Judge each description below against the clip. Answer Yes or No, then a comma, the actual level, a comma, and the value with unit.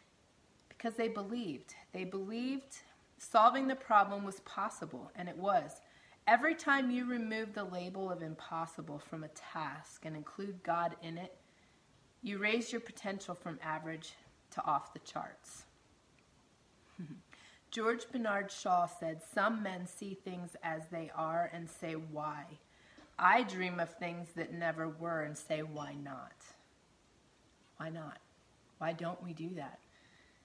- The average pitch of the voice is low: No, medium, 175 Hz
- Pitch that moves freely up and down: No, average, 4.1 semitones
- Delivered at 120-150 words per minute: Yes, average, 140 wpm